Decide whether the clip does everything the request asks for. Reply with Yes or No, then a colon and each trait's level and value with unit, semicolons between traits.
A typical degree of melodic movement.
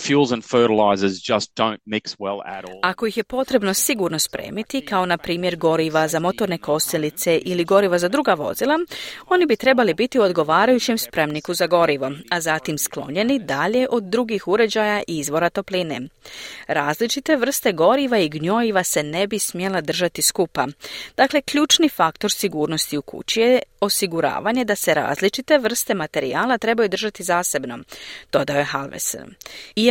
No: wide, 6.5 semitones